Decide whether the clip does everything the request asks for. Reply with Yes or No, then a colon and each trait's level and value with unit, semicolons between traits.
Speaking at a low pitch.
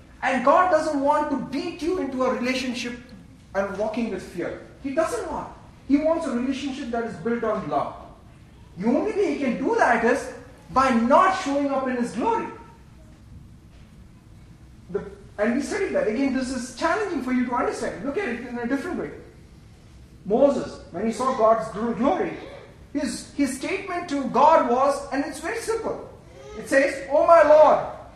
No: very high, 270 Hz